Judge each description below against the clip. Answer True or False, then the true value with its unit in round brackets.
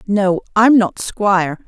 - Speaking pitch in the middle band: False (195 Hz)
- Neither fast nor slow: True (145 wpm)